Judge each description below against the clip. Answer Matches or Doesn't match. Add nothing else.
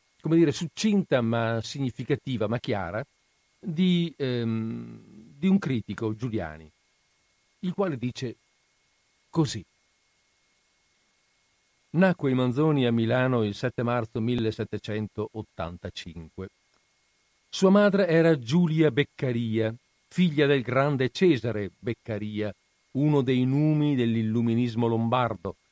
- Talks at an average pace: Doesn't match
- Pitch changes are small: Doesn't match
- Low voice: Matches